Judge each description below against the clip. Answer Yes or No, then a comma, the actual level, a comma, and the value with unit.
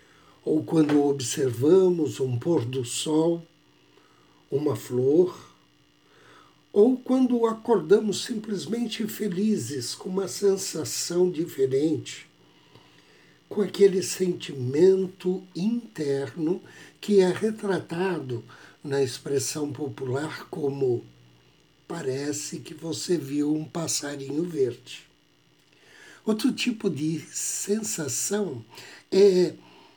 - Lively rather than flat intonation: Yes, wide, 5.8 semitones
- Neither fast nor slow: No, slow, 80 wpm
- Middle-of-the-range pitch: Yes, medium, 170 Hz